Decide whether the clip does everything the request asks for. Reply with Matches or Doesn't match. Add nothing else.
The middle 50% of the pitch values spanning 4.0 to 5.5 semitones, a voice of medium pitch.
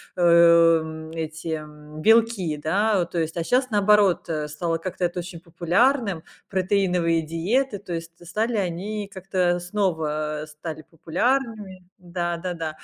Doesn't match